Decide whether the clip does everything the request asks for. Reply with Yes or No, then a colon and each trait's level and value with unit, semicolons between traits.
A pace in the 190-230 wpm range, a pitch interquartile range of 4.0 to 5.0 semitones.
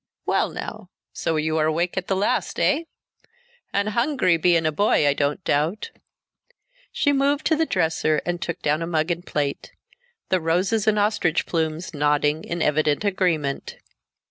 No: average, 165 wpm; average, 4.5 semitones